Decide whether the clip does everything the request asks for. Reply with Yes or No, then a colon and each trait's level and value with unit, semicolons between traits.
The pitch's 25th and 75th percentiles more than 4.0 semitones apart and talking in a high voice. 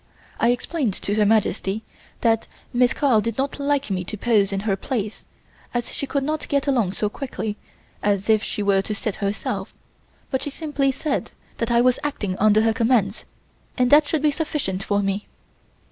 Yes: average, 5.0 semitones; high, 225 Hz